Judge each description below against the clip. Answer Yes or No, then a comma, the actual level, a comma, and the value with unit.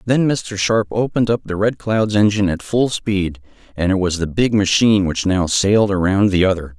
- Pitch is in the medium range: No, low, 100 Hz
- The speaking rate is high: Yes, fast, 210 wpm